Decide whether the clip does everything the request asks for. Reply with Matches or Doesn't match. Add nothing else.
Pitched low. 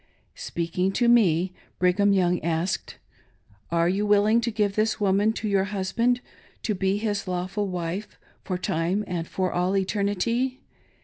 Doesn't match